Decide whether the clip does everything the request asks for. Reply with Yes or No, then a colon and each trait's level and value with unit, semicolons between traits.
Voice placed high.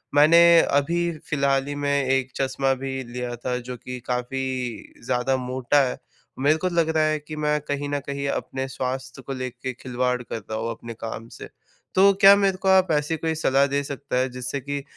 No: low, 135 Hz